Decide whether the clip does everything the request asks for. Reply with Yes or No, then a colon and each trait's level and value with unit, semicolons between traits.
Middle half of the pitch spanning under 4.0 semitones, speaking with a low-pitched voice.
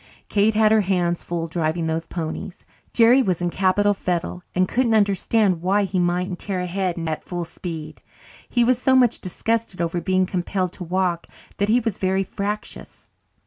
No: average, 3.0 semitones; medium, 185 Hz